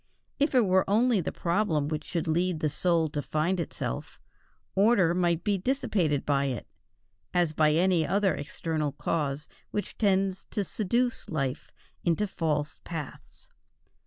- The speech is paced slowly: No, average, 145 wpm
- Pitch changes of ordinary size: Yes, average, 4.2 semitones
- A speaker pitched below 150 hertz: No, medium, 170 Hz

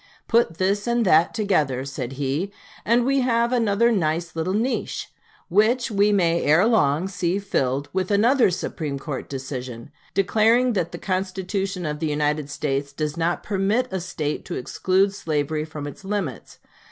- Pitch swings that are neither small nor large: No, wide, 5.7 semitones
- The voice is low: No, medium, 185 Hz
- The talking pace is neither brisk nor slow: Yes, average, 160 wpm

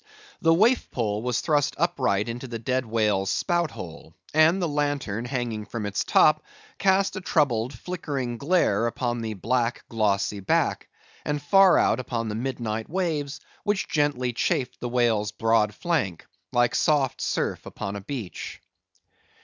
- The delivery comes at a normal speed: Yes, average, 150 wpm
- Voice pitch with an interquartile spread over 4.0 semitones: Yes, average, 5.1 semitones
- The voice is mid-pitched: No, low, 125 Hz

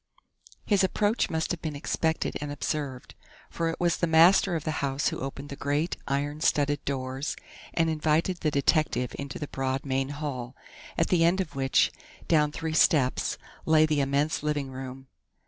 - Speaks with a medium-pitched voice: Yes, medium, 150 Hz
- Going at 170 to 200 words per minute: Yes, average, 175 wpm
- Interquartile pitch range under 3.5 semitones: Yes, average, 2.8 semitones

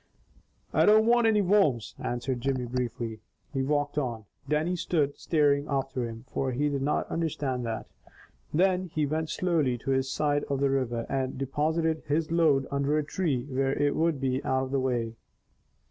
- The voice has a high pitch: No, medium, 140 Hz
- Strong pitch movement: No, average, 3.2 semitones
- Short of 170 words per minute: No, average, 175 wpm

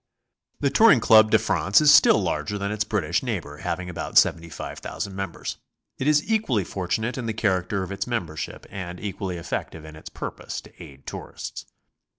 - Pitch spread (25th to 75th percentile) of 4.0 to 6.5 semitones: Yes, average, 4.5 semitones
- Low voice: Yes, low, 100 Hz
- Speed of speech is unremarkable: Yes, average, 170 wpm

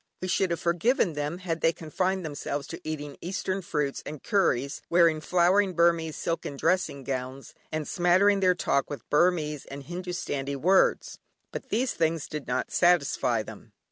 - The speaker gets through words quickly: No, average, 160 wpm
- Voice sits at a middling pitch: Yes, medium, 165 Hz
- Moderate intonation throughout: Yes, average, 4.1 semitones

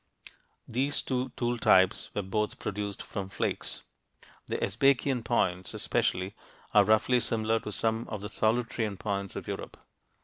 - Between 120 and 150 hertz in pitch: No, low, 110 Hz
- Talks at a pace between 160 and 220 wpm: No, average, 140 wpm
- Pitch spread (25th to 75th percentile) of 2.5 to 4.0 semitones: Yes, average, 3.2 semitones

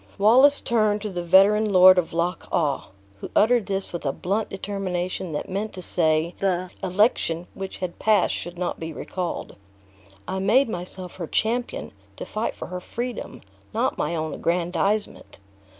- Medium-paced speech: Yes, average, 165 wpm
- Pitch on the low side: No, medium, 185 Hz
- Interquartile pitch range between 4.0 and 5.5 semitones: No, average, 3.3 semitones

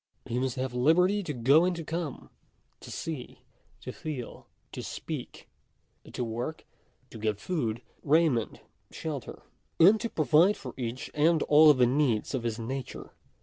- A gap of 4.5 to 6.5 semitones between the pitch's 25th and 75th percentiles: Yes, average, 4.9 semitones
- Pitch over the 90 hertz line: Yes, medium, 140 Hz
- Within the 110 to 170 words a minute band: Yes, average, 160 wpm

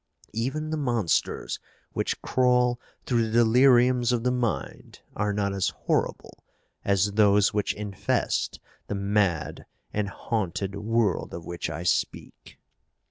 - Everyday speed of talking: No, slow, 130 wpm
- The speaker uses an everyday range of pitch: Yes, average, 3.6 semitones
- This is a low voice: Yes, low, 105 Hz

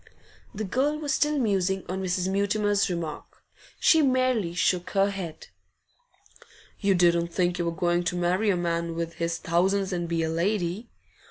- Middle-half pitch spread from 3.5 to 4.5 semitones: No, average, 3.1 semitones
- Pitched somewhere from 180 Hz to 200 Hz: Yes, medium, 185 Hz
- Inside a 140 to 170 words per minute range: Yes, average, 165 wpm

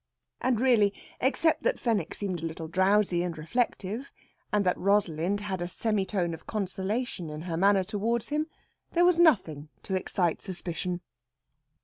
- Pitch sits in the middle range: No, high, 195 Hz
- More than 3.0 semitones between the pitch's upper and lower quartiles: Yes, average, 4.3 semitones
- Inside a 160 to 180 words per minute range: No, average, 150 wpm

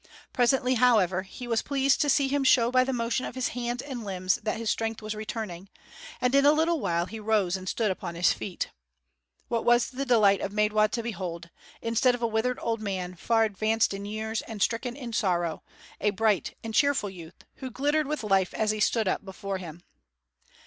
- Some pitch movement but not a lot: Yes, average, 4.1 semitones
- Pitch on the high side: Yes, high, 220 Hz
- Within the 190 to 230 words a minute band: Yes, fast, 205 wpm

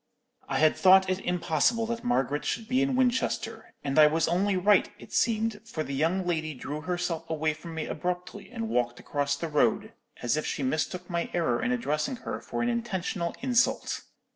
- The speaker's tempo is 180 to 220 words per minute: Yes, average, 190 wpm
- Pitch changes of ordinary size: No, wide, 6.4 semitones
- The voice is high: No, medium, 175 Hz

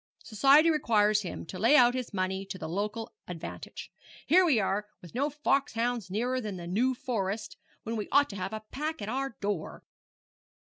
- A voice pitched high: Yes, high, 220 Hz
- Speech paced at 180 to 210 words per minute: Yes, average, 185 wpm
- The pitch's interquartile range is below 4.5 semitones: No, average, 4.9 semitones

